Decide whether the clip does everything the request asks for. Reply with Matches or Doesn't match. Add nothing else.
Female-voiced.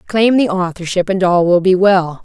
Matches